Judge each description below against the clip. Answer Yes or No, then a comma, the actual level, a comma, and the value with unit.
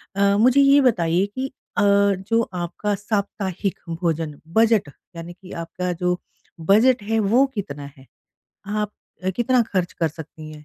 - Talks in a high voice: Yes, high, 200 Hz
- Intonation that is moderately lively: Yes, average, 4.5 semitones